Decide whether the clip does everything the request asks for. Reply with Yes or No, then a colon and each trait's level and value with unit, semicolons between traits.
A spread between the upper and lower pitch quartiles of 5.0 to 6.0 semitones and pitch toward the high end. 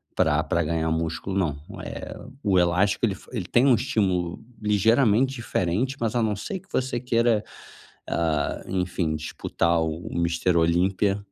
No: average, 5.3 semitones; very low, 95 Hz